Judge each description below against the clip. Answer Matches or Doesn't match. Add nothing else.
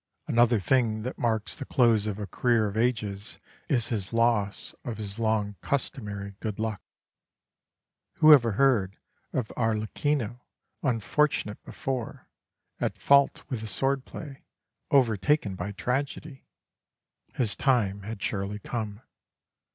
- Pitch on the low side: Matches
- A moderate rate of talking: Doesn't match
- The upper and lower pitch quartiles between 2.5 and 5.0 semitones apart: Matches